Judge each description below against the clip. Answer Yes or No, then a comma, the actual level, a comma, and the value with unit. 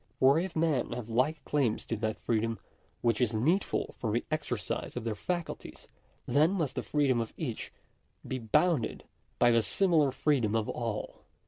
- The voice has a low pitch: Yes, low, 125 Hz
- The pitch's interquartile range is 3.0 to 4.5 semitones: No, average, 5.3 semitones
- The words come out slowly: No, average, 170 wpm